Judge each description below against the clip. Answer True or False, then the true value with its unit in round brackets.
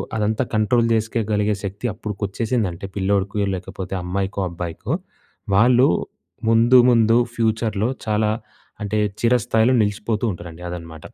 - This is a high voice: False (105 Hz)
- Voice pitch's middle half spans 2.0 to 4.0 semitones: True (2.7 semitones)